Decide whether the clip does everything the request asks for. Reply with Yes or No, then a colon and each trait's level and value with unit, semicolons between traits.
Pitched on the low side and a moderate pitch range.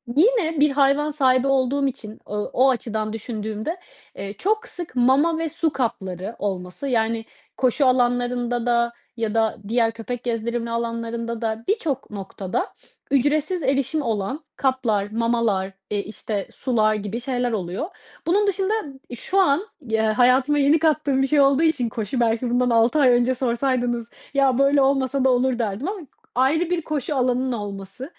No: very high, 250 Hz; average, 3.7 semitones